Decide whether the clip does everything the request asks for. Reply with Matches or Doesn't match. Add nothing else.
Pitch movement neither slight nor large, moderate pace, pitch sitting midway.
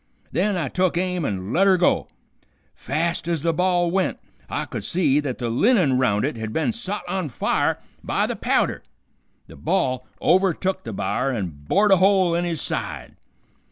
Doesn't match